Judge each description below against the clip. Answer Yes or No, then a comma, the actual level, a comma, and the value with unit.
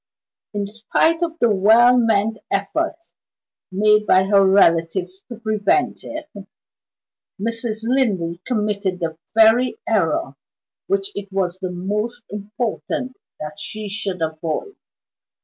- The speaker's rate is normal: No, slow, 115 wpm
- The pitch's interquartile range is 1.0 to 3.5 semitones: No, average, 4.0 semitones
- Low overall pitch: No, high, 210 Hz